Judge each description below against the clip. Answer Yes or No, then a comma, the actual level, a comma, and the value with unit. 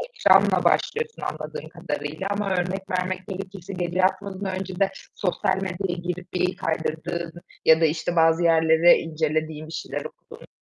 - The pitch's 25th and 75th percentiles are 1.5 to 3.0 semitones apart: Yes, narrow, 2.5 semitones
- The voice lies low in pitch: No, medium, 180 Hz